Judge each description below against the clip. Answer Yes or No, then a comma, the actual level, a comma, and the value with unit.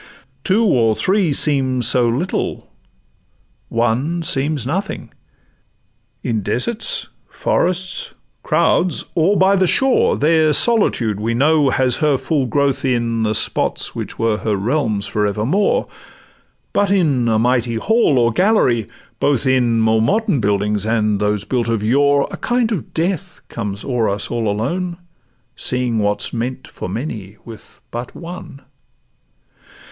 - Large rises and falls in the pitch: Yes, wide, 6.7 semitones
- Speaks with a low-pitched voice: Yes, low, 130 Hz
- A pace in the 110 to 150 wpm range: Yes, average, 140 wpm